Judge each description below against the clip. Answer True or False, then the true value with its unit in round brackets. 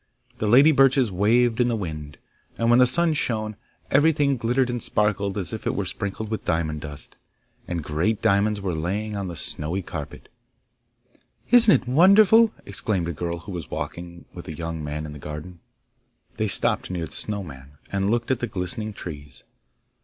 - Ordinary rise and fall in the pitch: False (6.1 semitones)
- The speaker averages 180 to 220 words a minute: True (185 wpm)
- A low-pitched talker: True (100 Hz)